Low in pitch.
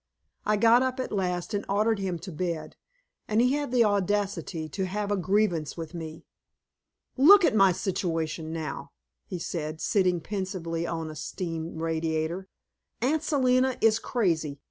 No: medium, 185 Hz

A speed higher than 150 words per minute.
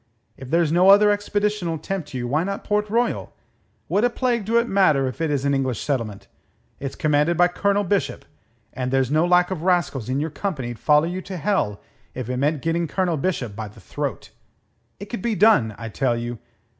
Yes: fast, 205 wpm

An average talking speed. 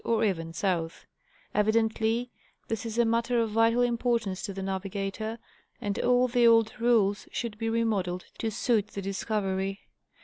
Yes: average, 150 wpm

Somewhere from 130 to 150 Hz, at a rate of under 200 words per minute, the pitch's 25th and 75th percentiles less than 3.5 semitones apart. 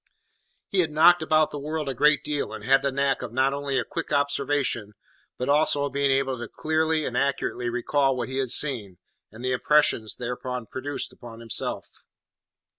Yes: low, 135 Hz; average, 190 wpm; average, 2.9 semitones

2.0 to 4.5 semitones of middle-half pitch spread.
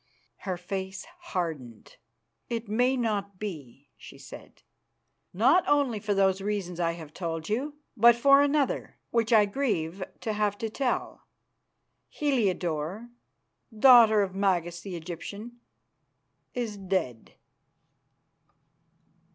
No: average, 5.1 semitones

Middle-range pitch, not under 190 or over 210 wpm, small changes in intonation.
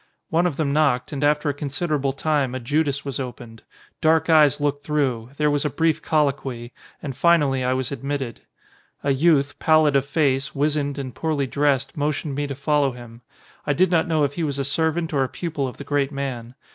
Yes: medium, 145 Hz; fast, 205 wpm; narrow, 2.2 semitones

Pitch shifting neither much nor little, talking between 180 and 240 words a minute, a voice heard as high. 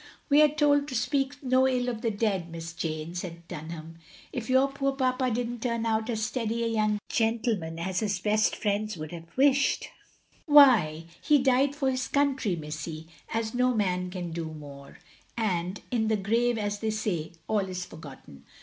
No: wide, 6.7 semitones; average, 185 wpm; high, 220 Hz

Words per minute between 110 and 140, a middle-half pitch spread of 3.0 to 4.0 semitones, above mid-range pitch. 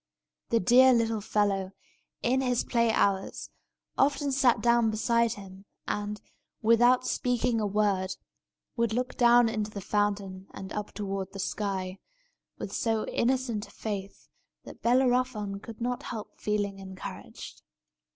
Yes: slow, 135 wpm; average, 3.3 semitones; high, 215 Hz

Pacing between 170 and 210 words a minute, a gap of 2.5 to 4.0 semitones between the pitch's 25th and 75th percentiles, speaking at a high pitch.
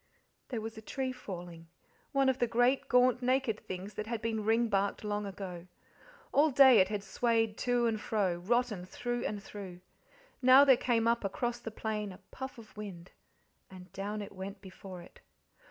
Yes: average, 180 wpm; average, 3.7 semitones; high, 220 Hz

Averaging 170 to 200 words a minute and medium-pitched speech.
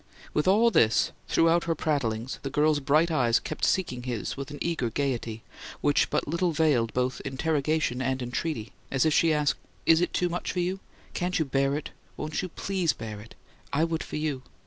Yes: average, 195 wpm; medium, 150 Hz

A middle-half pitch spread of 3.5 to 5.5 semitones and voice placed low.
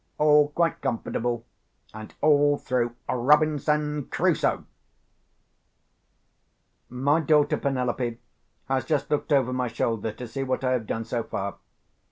Yes: average, 3.8 semitones; low, 130 Hz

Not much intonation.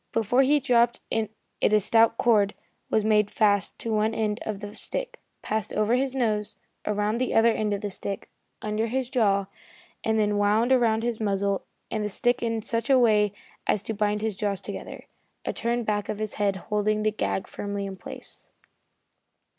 Yes: narrow, 1.9 semitones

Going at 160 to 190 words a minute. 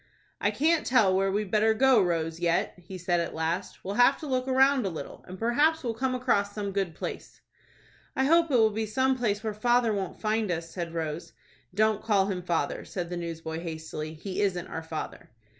No: fast, 205 wpm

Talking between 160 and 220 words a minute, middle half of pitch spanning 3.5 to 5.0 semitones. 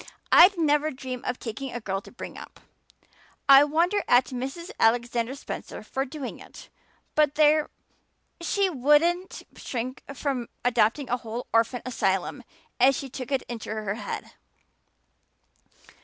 No: average, 140 wpm; average, 3.8 semitones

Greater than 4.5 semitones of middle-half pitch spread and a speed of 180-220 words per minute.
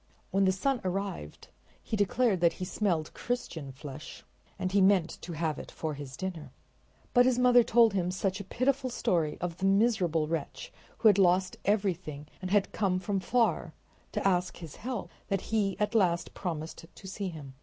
No: average, 3.8 semitones; average, 185 wpm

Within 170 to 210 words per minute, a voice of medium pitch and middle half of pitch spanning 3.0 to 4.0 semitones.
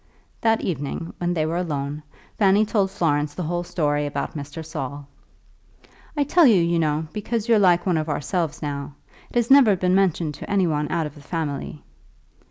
No: average, 185 wpm; medium, 165 Hz; average, 4.6 semitones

